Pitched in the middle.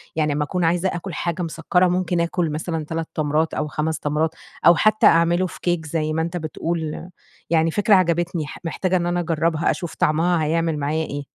Yes: medium, 165 Hz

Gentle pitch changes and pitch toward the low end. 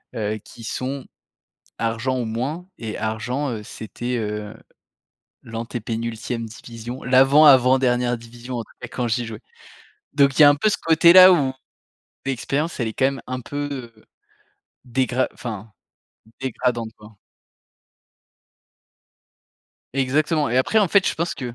No: average, 3.3 semitones; low, 125 Hz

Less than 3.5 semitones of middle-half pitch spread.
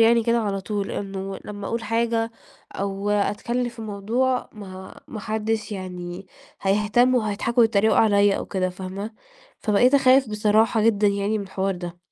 Yes: narrow, 2.6 semitones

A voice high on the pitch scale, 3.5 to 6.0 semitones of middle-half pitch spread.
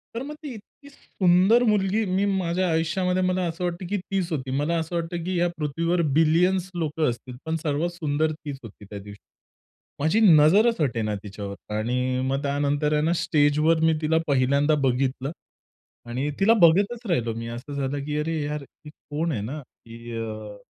No: medium, 155 Hz; average, 4.8 semitones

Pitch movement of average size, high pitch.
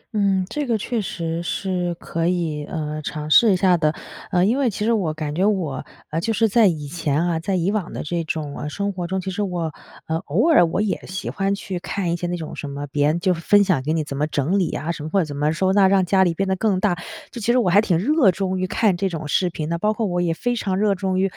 No: average, 3.7 semitones; medium, 180 Hz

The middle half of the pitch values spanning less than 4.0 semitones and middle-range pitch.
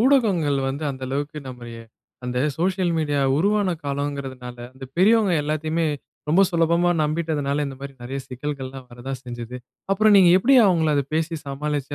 No: average, 4.3 semitones; medium, 150 Hz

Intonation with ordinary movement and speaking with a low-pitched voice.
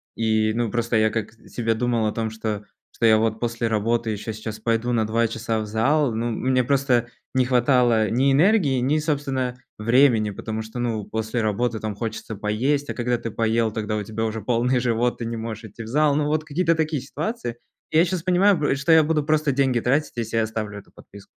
Yes: average, 3.6 semitones; low, 115 Hz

